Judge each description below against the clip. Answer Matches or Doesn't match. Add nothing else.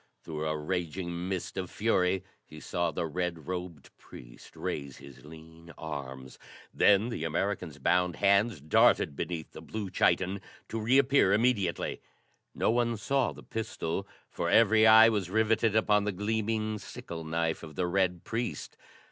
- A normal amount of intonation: Matches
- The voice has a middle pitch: Doesn't match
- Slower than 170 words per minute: Matches